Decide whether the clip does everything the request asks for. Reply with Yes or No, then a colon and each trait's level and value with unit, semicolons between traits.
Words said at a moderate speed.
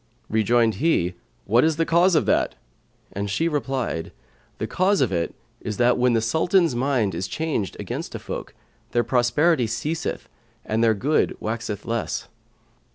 Yes: average, 160 wpm